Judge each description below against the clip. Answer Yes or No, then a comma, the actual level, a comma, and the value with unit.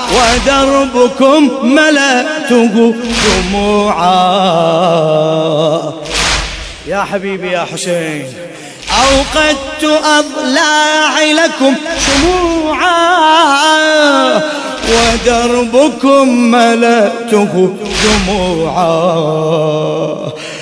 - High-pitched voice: Yes, high, 235 Hz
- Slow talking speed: Yes, slow, 40 wpm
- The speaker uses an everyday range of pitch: No, wide, 8.6 semitones